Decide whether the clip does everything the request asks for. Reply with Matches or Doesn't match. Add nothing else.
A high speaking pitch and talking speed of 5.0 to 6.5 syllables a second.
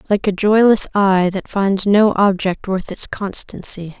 Doesn't match